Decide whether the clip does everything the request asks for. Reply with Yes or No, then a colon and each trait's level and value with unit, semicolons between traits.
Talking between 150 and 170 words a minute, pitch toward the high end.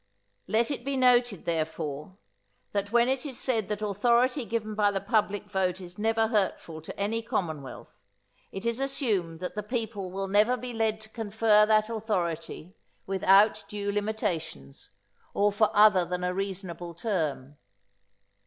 Yes: average, 155 wpm; high, 205 Hz